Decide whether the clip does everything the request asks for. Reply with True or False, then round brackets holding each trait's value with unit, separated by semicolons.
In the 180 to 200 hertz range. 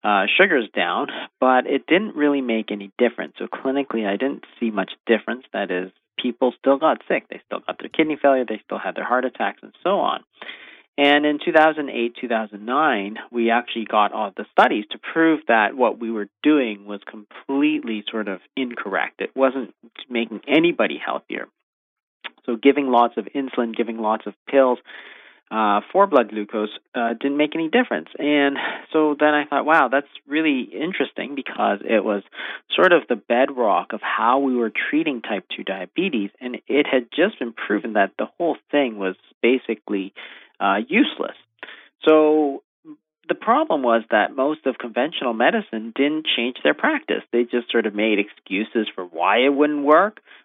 False (125 Hz)